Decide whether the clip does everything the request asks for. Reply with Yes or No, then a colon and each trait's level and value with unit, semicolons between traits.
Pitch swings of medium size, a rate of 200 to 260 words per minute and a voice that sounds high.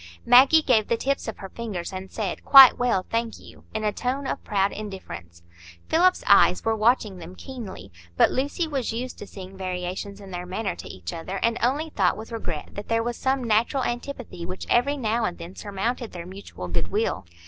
Yes: average, 4.8 semitones; fast, 205 wpm; high, 215 Hz